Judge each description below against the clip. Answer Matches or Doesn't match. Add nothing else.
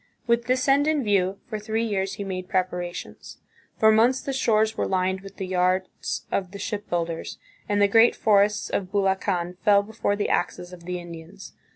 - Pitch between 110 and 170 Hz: Doesn't match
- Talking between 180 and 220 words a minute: Matches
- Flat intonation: Doesn't match